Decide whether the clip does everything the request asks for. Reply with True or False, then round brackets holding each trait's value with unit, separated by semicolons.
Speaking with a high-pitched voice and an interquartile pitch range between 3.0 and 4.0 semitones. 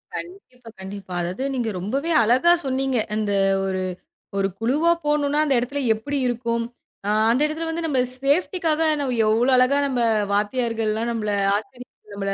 False (250 Hz; 4.7 semitones)